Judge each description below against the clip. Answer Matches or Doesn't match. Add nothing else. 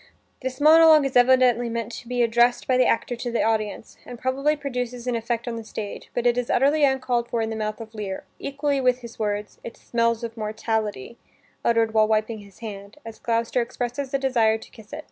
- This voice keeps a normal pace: Doesn't match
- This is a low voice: Doesn't match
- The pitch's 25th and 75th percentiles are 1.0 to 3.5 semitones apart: Matches